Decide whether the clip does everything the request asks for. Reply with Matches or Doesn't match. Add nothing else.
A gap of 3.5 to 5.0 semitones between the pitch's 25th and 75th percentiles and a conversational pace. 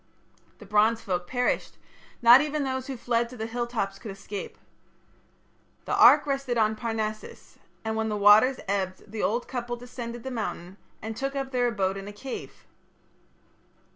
Doesn't match